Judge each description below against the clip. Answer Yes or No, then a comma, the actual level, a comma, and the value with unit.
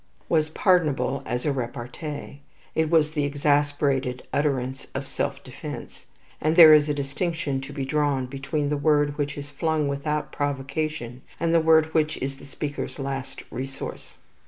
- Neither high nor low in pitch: Yes, medium, 145 Hz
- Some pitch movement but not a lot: No, narrow, 2.2 semitones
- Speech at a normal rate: Yes, average, 160 wpm